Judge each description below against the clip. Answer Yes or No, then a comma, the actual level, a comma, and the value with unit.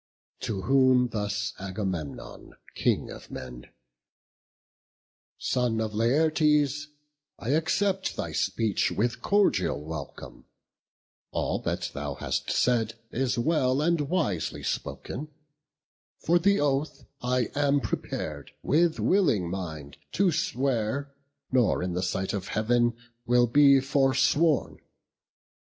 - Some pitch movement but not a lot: No, wide, 6.4 semitones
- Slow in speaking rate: Yes, slow, 110 wpm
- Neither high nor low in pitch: No, low, 125 Hz